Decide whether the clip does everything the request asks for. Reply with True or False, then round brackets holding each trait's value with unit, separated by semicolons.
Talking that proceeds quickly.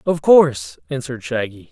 False (140 wpm)